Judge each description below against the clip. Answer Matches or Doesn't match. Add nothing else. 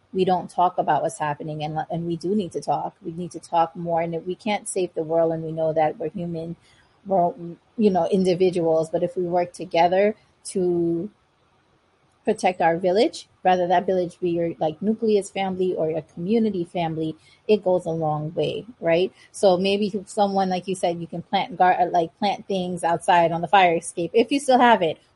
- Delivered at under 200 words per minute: Doesn't match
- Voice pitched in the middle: Matches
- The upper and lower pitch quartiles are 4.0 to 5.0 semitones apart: Doesn't match